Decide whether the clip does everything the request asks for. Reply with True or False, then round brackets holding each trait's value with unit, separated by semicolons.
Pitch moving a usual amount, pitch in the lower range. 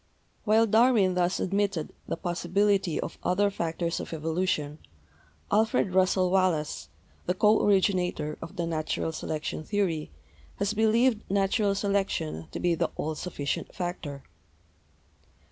False (3.8 semitones; 185 Hz)